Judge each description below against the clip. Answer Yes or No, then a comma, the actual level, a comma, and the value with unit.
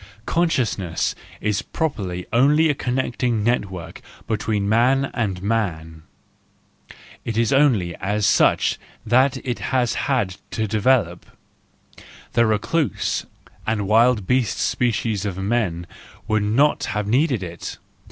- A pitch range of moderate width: Yes, average, 4.1 semitones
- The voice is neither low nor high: No, low, 110 Hz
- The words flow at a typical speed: No, slow, 115 wpm